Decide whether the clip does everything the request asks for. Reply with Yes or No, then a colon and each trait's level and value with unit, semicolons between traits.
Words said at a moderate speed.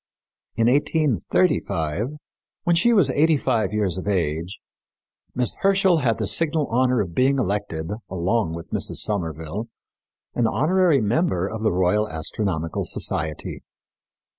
No: slow, 130 wpm